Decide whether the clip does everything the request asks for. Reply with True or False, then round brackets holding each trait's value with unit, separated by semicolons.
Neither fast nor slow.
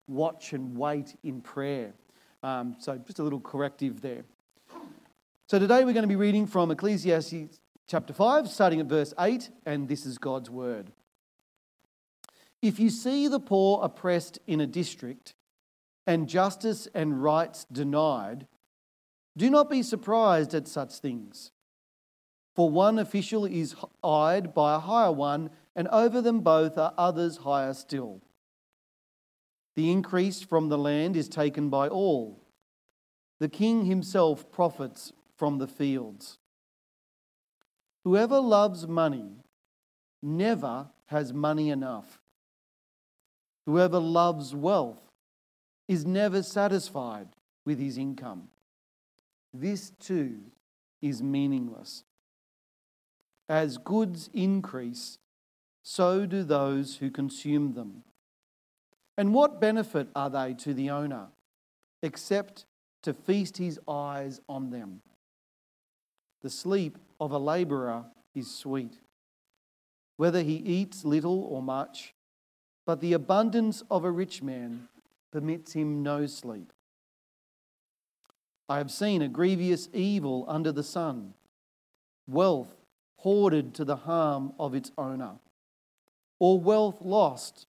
False (120 wpm)